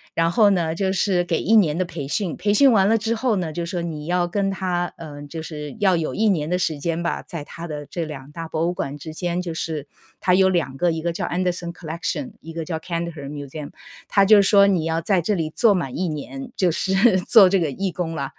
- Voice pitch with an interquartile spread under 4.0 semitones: Yes, average, 3.2 semitones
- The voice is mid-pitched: Yes, medium, 170 Hz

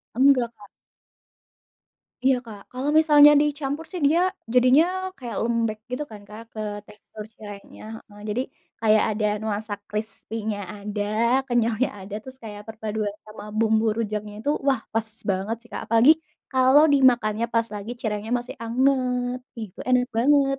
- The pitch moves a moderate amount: Yes, average, 3.4 semitones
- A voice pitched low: No, high, 230 Hz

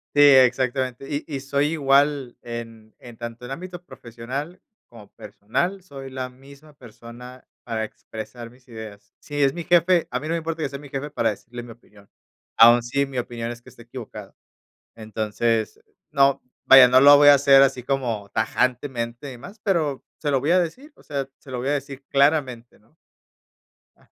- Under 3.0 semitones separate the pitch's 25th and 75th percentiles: No, average, 3.4 semitones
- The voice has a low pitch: Yes, low, 130 Hz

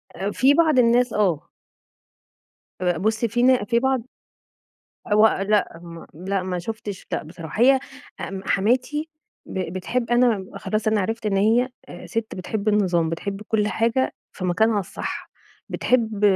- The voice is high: Yes, high, 215 Hz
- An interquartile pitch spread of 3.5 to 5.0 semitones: Yes, average, 4.1 semitones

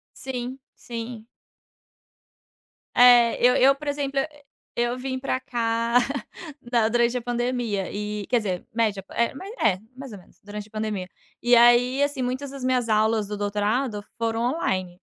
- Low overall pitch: No, high, 235 Hz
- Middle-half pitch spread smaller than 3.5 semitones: Yes, average, 3.1 semitones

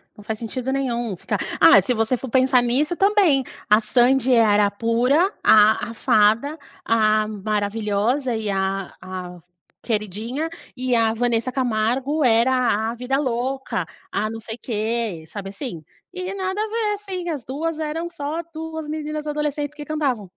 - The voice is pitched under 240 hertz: No, high, 245 Hz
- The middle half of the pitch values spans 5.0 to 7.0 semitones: Yes, wide, 5.5 semitones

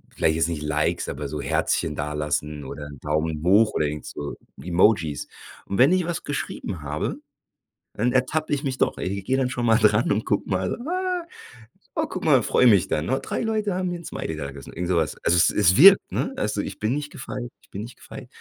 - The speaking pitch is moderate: No, low, 100 Hz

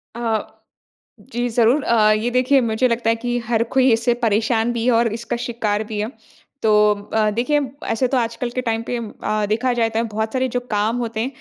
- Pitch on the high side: Yes, high, 230 Hz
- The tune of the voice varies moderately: No, narrow, 1.7 semitones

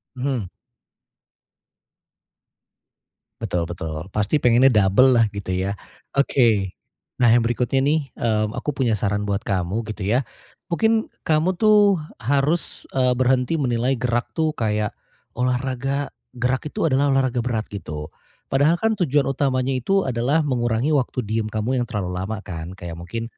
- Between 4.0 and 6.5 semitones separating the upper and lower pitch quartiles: Yes, average, 4.5 semitones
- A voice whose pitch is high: No, low, 125 Hz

